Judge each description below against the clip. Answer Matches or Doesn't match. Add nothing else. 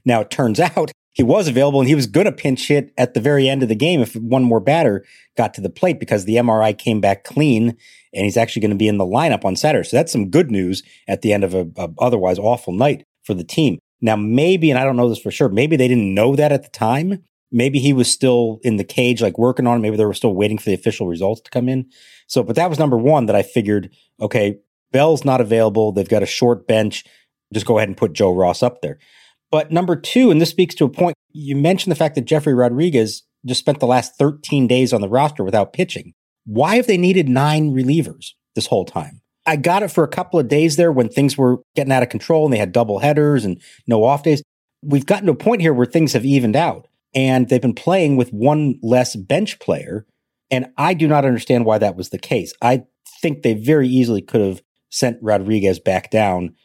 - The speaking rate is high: Matches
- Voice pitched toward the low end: Matches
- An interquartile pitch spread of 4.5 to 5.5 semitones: Matches